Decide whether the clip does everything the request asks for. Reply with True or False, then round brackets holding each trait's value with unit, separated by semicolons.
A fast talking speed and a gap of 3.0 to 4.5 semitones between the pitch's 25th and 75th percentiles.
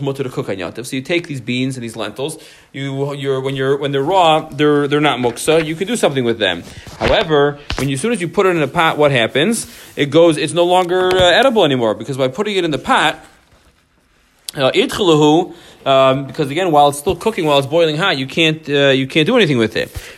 True (225 wpm; 3.5 semitones)